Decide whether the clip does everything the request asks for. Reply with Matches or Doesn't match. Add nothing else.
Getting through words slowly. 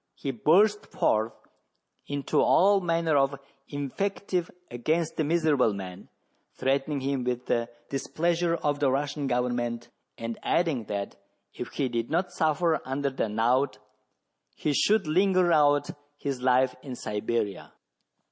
Matches